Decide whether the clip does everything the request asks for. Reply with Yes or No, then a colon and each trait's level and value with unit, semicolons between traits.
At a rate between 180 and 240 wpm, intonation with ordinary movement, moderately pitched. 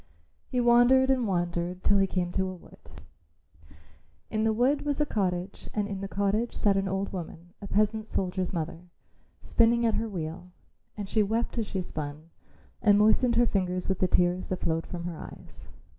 No: average, 190 wpm; average, 3.8 semitones; high, 195 Hz